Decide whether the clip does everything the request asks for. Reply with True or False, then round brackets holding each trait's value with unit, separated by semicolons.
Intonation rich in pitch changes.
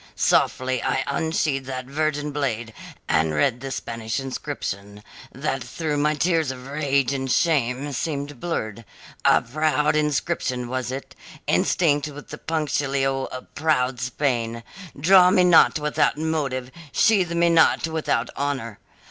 False (3.4 semitones)